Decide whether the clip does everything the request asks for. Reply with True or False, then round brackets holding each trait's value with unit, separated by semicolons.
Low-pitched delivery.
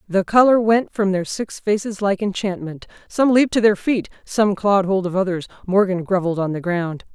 False (195 Hz)